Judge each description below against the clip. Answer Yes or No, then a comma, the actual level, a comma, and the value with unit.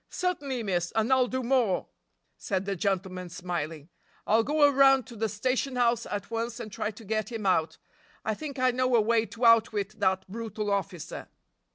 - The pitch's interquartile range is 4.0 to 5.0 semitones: Yes, average, 4.4 semitones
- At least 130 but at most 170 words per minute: No, average, 185 wpm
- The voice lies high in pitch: Yes, high, 220 Hz